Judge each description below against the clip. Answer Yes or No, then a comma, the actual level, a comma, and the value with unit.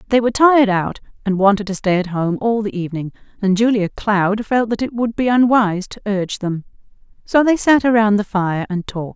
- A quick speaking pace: Yes, fast, 215 wpm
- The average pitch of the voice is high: Yes, high, 210 Hz